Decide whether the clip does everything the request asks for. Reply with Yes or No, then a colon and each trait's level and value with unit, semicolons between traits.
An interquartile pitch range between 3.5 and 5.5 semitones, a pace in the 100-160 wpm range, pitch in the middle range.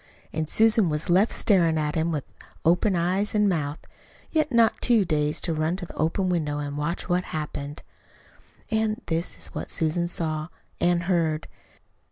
No: average, 3.8 semitones; average, 170 wpm; medium, 170 Hz